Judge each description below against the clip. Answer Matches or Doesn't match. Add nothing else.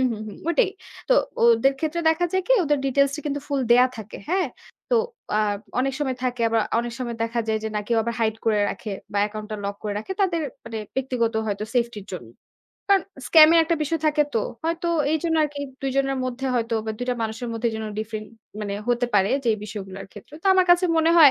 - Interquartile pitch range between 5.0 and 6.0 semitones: Matches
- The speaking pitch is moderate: Doesn't match